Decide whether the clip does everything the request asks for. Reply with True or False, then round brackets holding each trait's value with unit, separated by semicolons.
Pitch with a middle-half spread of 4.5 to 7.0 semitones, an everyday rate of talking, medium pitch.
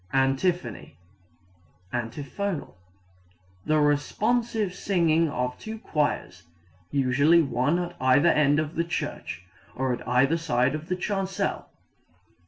False (5.1 semitones; 110 wpm; 150 Hz)